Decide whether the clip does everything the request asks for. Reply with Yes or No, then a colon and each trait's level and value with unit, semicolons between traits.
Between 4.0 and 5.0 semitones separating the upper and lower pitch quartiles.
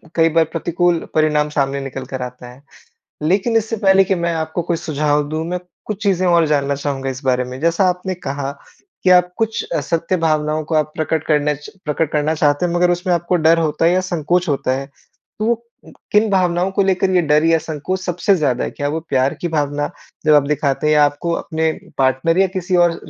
No: average, 3.5 semitones